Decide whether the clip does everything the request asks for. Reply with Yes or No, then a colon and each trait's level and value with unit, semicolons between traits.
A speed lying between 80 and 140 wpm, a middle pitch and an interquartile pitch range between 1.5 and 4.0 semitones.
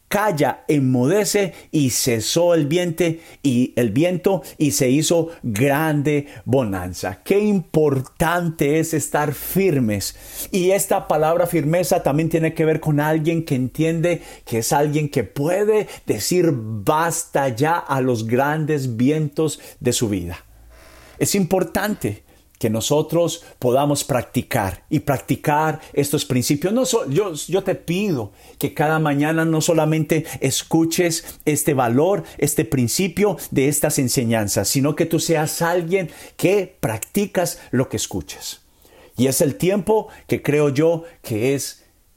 No: average, 135 wpm; medium, 150 Hz; average, 4.4 semitones